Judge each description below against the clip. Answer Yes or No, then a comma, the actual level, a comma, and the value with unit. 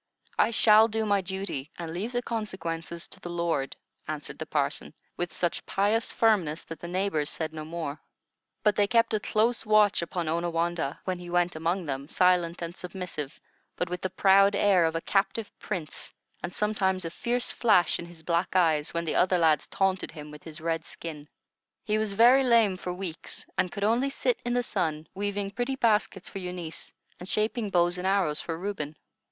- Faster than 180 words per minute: Yes, average, 190 wpm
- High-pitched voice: No, medium, 180 Hz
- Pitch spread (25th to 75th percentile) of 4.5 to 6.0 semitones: No, average, 3.9 semitones